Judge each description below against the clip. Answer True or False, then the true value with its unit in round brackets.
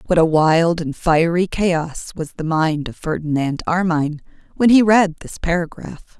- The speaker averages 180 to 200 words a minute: False (165 wpm)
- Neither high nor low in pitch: True (165 Hz)